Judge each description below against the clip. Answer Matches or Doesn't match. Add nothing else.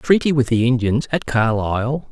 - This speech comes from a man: Matches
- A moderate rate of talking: Matches